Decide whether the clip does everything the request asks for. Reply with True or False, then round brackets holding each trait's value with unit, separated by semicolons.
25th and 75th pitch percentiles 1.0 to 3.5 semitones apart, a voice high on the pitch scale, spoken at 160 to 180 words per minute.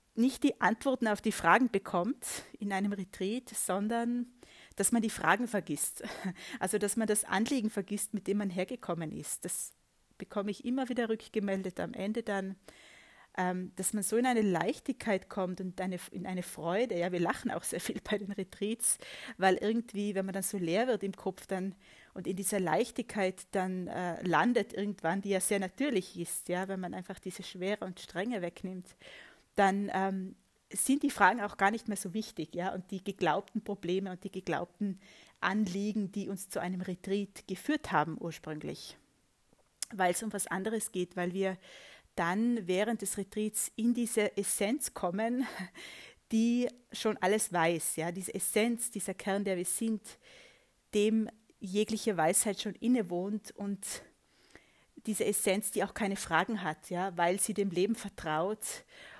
True (2.9 semitones; 200 Hz; 170 wpm)